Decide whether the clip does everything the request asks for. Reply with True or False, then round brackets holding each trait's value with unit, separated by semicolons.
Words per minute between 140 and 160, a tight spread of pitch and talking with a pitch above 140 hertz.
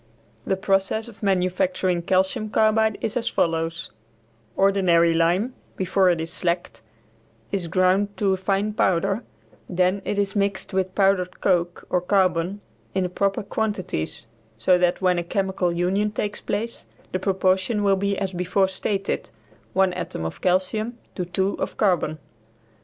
True (150 wpm; 1.9 semitones; 190 Hz)